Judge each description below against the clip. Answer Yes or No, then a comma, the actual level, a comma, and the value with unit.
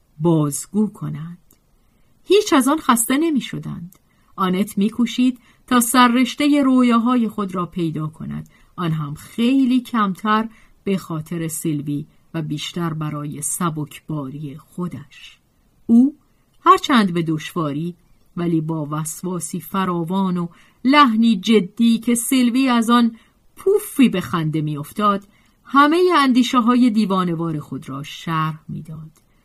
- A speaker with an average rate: Yes, average, 120 wpm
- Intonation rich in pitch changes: Yes, wide, 7.5 semitones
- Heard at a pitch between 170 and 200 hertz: Yes, high, 190 Hz